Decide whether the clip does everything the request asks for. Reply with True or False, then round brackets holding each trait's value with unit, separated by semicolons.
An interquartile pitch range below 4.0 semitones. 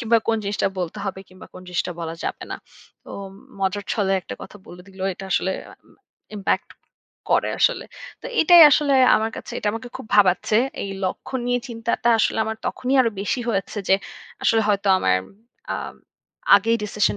True (3.2 semitones)